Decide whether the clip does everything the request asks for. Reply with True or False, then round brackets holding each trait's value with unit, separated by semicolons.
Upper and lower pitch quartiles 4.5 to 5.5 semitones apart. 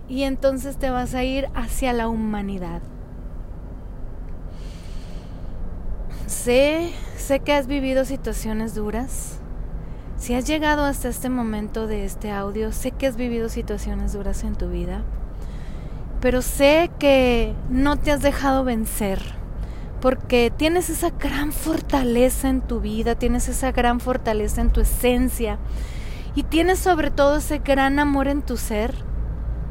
True (4.8 semitones)